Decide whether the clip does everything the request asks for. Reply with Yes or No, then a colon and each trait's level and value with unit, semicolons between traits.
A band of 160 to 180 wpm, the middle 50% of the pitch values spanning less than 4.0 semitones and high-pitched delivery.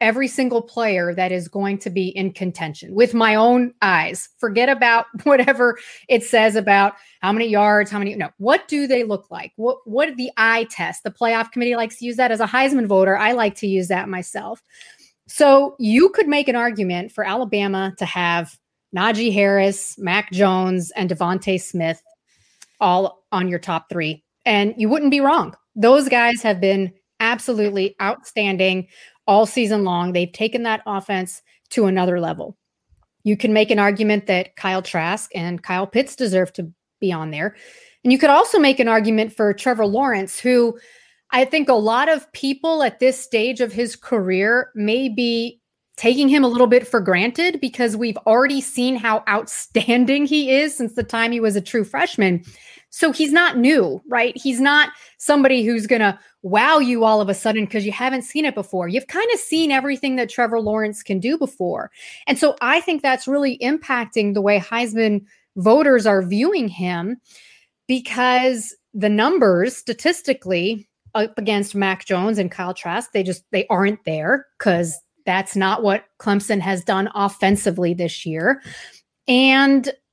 No: average, 175 wpm; average, 4.5 semitones; high, 225 Hz